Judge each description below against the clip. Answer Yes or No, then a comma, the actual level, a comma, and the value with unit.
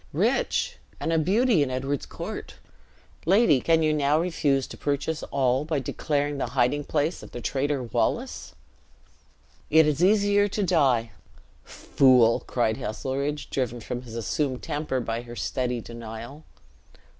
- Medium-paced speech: Yes, average, 145 wpm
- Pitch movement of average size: Yes, average, 4.0 semitones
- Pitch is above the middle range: No, medium, 140 Hz